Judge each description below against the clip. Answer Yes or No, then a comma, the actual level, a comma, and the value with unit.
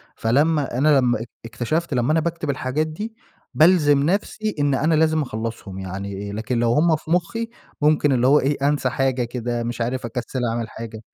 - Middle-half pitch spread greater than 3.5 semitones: Yes, average, 4.8 semitones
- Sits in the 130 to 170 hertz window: Yes, low, 135 Hz